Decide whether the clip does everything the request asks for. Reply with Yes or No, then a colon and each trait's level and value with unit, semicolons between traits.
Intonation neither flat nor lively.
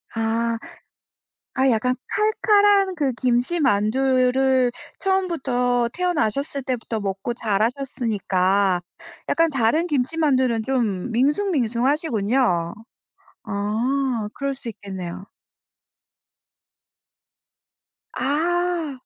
Yes: average, 4.4 semitones